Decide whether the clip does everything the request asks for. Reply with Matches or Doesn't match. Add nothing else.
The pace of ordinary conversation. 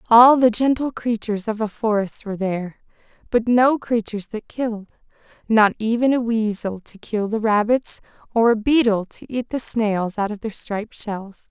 Matches